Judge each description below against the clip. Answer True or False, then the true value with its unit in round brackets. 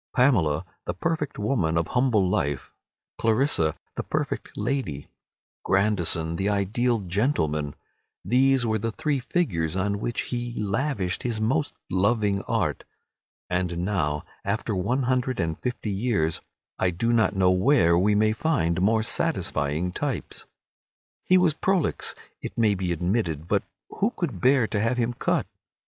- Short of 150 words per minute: True (140 wpm)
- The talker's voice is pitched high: False (105 Hz)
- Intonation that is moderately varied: False (5.7 semitones)